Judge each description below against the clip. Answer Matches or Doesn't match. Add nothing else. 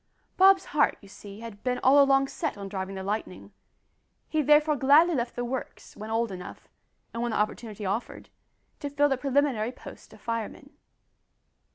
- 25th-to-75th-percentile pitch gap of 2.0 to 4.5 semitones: Doesn't match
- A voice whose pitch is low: Doesn't match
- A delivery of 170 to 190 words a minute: Matches